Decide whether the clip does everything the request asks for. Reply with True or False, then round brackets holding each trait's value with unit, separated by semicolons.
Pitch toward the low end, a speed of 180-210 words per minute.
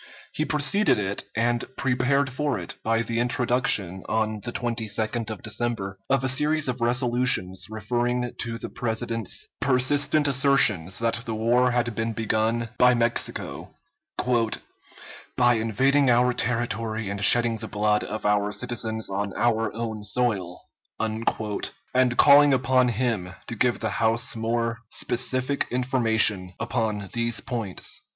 False (115 Hz; 135 wpm)